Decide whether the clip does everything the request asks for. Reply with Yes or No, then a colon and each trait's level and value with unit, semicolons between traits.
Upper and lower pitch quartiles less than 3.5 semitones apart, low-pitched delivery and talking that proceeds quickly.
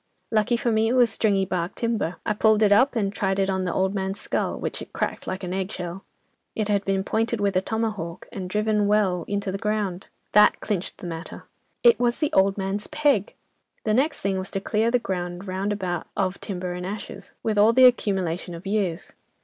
No: narrow, 2.6 semitones; high, 200 Hz; fast, 215 wpm